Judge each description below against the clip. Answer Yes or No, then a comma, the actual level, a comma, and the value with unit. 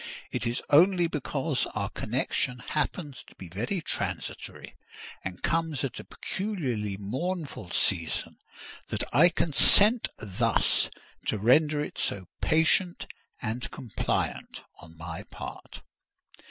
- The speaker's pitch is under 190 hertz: Yes, low, 135 Hz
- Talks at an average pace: No, slow, 115 wpm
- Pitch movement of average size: No, wide, 7.9 semitones